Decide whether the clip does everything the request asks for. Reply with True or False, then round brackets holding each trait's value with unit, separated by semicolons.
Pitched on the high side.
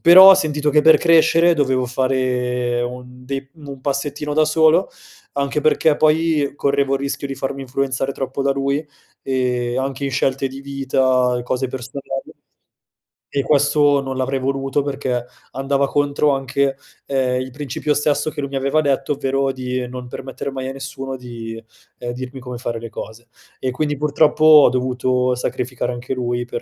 False (135 Hz)